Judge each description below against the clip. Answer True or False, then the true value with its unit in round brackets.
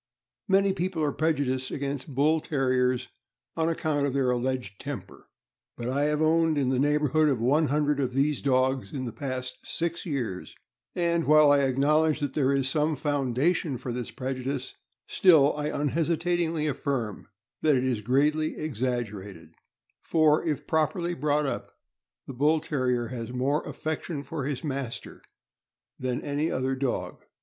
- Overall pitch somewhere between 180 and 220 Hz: False (140 Hz)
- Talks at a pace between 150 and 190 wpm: True (155 wpm)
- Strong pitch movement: False (3.2 semitones)